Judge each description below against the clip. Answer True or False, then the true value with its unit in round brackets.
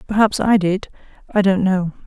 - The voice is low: False (195 Hz)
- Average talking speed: True (145 wpm)